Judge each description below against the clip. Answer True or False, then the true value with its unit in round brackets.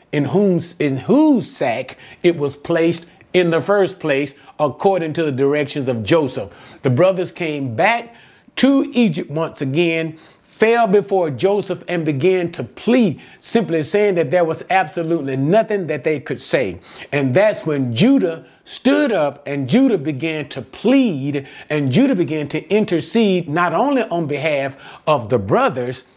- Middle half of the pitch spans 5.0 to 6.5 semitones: True (5.4 semitones)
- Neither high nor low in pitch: True (165 Hz)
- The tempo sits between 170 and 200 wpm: False (155 wpm)